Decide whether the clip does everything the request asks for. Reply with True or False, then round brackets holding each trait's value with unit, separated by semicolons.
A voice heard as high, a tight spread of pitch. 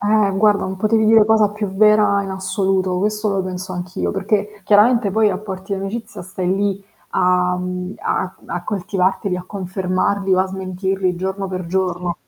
True (195 Hz; 2.1 semitones)